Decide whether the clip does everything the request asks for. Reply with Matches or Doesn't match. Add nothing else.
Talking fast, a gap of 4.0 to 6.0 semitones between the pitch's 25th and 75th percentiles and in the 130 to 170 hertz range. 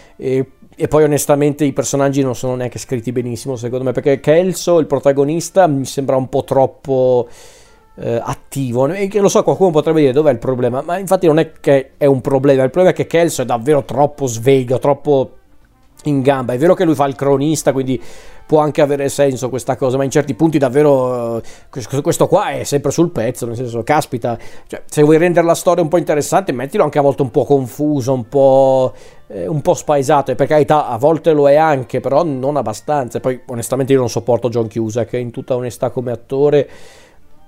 Doesn't match